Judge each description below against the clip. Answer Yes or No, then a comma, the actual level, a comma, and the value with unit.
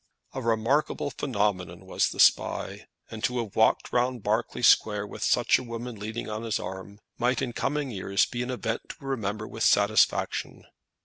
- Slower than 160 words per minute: No, average, 175 wpm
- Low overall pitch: Yes, low, 115 Hz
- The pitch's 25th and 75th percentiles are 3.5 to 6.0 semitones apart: No, average, 2.9 semitones